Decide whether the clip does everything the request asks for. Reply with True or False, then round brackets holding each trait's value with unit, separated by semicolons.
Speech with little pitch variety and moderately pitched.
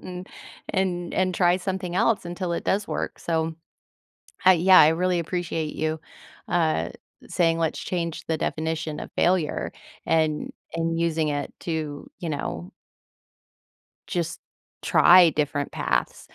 True (2.2 semitones; 165 Hz)